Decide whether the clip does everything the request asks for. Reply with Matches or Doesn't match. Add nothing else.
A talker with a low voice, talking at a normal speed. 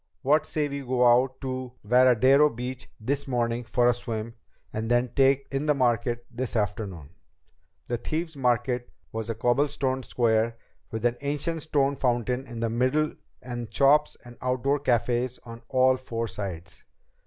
Matches